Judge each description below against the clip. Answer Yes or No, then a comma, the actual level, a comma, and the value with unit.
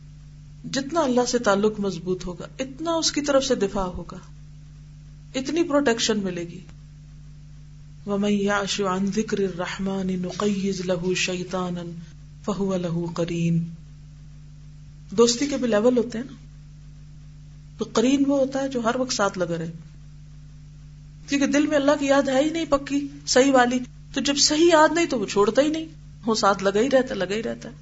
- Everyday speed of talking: Yes, average, 160 wpm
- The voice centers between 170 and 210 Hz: Yes, high, 190 Hz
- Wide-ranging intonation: Yes, wide, 8.9 semitones